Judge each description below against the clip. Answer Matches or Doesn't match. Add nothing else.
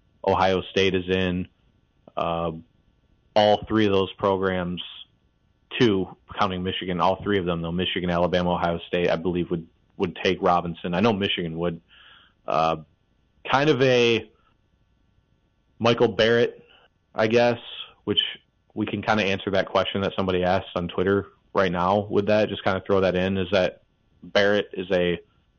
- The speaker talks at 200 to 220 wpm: Doesn't match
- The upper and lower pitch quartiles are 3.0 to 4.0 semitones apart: Doesn't match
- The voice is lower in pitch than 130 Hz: Matches